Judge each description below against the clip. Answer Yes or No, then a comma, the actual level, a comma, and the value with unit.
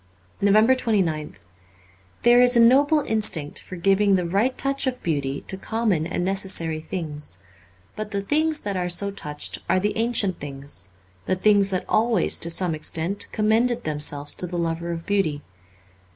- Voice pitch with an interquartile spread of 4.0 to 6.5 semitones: Yes, average, 5.2 semitones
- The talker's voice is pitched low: No, high, 190 Hz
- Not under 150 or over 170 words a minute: Yes, average, 165 wpm